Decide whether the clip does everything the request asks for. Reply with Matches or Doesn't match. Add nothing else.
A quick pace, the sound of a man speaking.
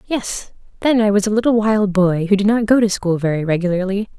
Doesn't match